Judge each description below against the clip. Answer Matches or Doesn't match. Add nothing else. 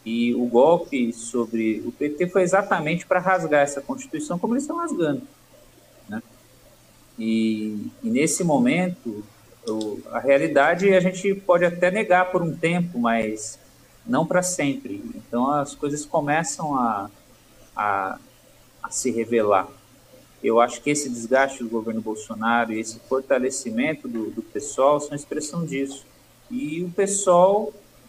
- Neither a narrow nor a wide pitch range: Doesn't match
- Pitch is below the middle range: Doesn't match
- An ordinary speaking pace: Matches